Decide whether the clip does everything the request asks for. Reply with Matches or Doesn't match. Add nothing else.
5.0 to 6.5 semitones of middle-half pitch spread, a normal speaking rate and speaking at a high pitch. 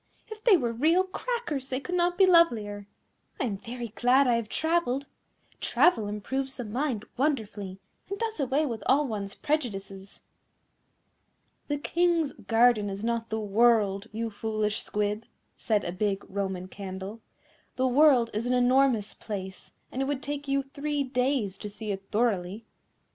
Matches